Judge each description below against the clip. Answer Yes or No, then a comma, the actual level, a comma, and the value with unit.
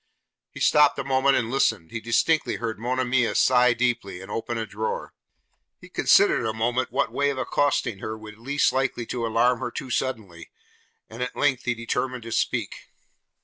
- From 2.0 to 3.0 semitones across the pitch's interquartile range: Yes, average, 2.7 semitones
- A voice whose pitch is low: Yes, low, 120 Hz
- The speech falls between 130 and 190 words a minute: Yes, average, 180 wpm